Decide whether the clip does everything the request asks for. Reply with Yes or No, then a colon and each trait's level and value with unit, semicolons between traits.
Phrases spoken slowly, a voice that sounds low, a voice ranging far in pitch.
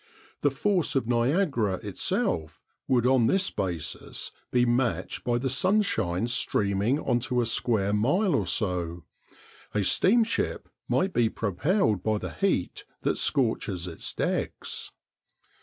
Yes: slow, 130 wpm; low, 120 Hz; wide, 6.2 semitones